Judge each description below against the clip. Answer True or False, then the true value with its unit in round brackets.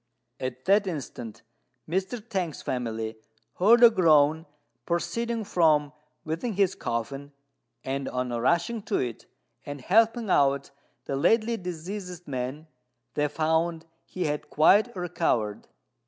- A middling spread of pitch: False (6.0 semitones)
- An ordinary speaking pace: False (120 wpm)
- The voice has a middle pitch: True (160 Hz)